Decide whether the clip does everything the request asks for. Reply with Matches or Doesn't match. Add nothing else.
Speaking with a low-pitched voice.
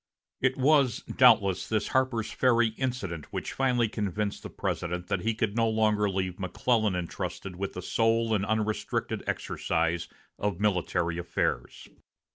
Matches